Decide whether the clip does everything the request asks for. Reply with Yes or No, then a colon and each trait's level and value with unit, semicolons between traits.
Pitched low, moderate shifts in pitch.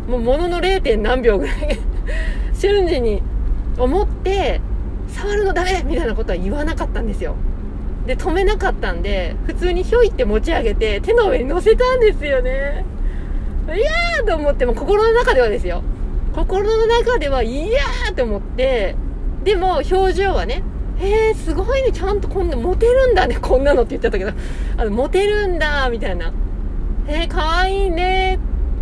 No: very high, 380 Hz; average, 4.5 semitones